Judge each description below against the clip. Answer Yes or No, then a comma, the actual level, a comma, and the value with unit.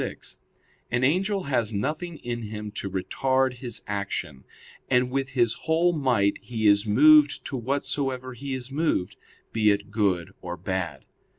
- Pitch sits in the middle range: No, low, 125 Hz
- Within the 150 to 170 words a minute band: Yes, average, 155 wpm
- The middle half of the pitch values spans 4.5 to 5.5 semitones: Yes, average, 5.2 semitones